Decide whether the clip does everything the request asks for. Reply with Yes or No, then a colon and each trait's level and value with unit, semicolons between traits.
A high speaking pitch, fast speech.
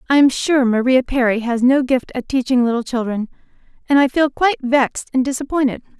No: very high, 260 Hz; average, 190 wpm